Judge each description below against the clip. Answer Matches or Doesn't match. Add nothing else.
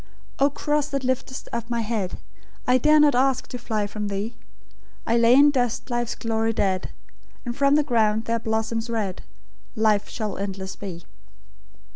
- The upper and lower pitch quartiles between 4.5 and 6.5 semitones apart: Doesn't match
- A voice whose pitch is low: Doesn't match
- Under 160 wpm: Doesn't match